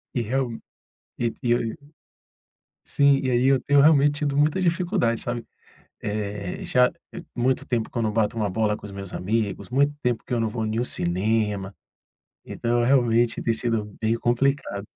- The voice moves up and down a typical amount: Yes, average, 3.9 semitones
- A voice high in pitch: No, low, 120 Hz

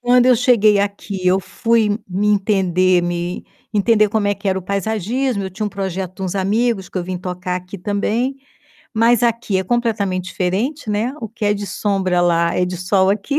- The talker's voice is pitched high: Yes, high, 200 Hz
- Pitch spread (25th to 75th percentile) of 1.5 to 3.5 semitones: Yes, average, 3.2 semitones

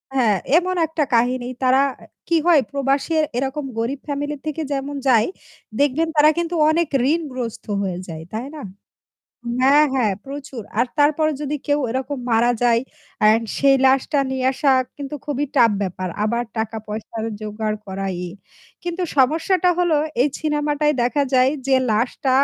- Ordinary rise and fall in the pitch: Yes, average, 4.1 semitones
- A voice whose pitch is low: No, very high, 270 Hz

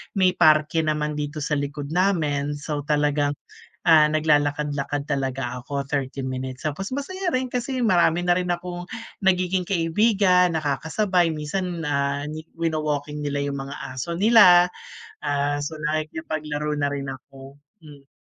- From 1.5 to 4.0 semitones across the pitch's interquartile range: Yes, average, 3.6 semitones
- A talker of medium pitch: Yes, medium, 150 Hz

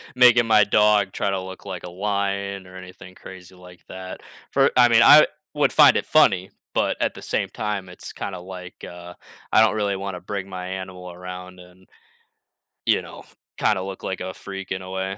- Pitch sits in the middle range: No, very low, 95 Hz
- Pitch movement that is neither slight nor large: No, narrow, 1.8 semitones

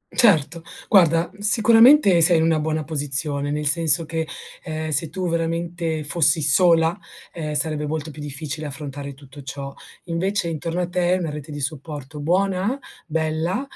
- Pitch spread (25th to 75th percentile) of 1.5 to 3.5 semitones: Yes, average, 2.7 semitones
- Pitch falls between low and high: Yes, medium, 160 Hz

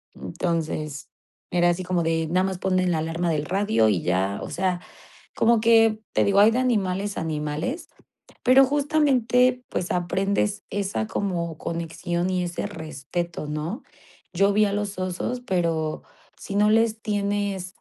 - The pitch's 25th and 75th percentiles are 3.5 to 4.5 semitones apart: Yes, average, 4.0 semitones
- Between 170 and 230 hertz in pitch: Yes, medium, 185 Hz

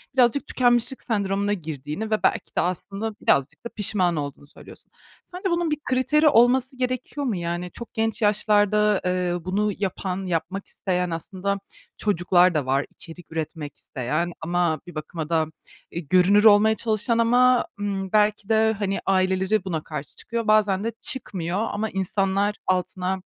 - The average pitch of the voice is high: Yes, high, 195 Hz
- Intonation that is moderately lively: Yes, average, 3.9 semitones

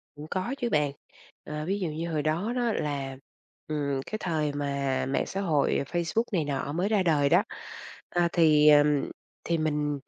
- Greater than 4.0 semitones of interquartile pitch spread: No, average, 3.3 semitones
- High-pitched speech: No, medium, 155 Hz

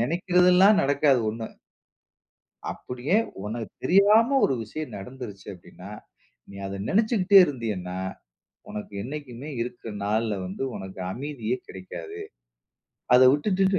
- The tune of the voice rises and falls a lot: Yes, wide, 9.0 semitones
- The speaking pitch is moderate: No, low, 125 Hz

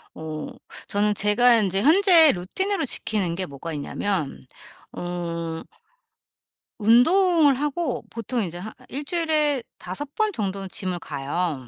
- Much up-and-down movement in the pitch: Yes, wide, 8.8 semitones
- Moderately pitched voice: No, high, 210 Hz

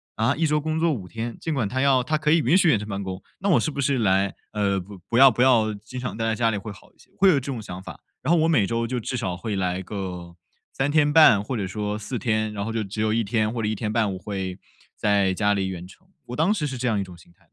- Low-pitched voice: Yes, low, 110 Hz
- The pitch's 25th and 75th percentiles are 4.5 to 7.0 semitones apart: Yes, average, 5.2 semitones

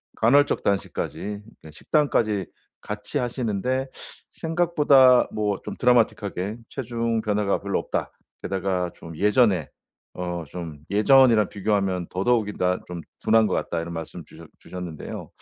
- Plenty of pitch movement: No, average, 5.0 semitones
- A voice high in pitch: No, low, 105 Hz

